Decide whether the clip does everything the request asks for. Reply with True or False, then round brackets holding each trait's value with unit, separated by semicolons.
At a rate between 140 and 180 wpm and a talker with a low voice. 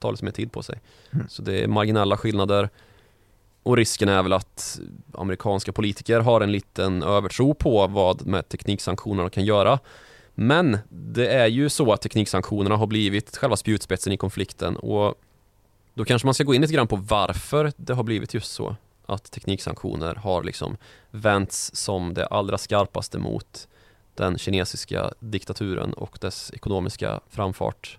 True (160 wpm; 105 Hz)